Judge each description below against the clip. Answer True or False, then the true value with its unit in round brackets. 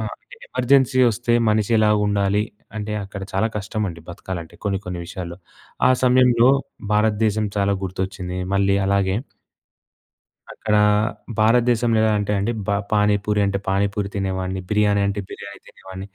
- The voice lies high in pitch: False (100 Hz)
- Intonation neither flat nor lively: False (2.0 semitones)